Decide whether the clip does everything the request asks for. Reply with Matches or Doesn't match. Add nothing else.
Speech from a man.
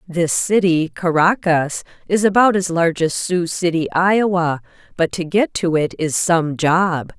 Doesn't match